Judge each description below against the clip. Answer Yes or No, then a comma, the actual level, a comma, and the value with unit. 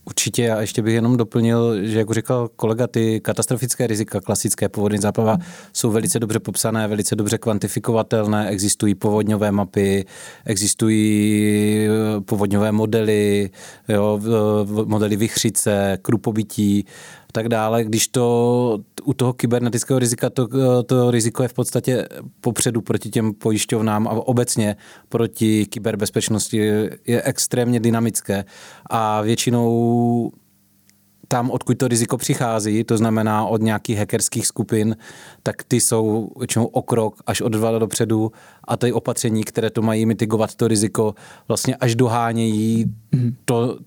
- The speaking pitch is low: Yes, low, 115 Hz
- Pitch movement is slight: Yes, narrow, 1.9 semitones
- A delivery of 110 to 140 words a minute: Yes, average, 130 wpm